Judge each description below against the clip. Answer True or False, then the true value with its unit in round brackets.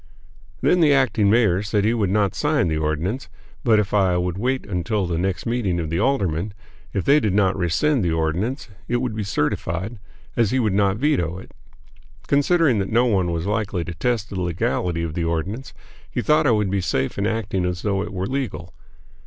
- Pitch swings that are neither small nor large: True (4.9 semitones)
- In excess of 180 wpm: True (205 wpm)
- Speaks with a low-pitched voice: True (100 Hz)